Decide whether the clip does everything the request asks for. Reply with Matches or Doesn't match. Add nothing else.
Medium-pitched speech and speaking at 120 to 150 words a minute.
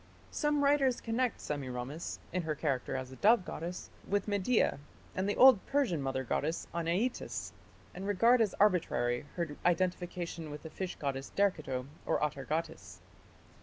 Matches